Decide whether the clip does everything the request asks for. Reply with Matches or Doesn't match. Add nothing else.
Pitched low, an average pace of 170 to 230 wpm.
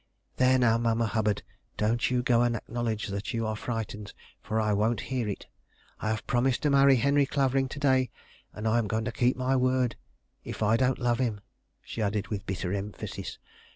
Matches